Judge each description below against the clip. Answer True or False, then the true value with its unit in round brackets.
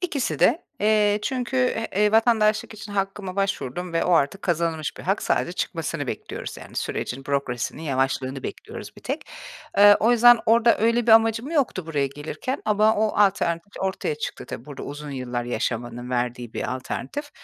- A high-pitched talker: True (195 Hz)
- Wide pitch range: True (8.3 semitones)